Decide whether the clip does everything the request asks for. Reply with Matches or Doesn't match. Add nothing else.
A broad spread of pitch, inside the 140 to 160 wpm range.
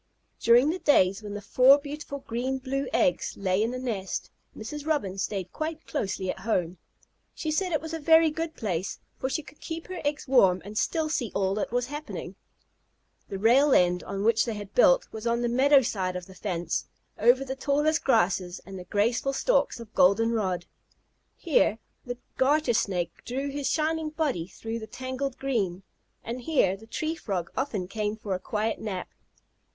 Doesn't match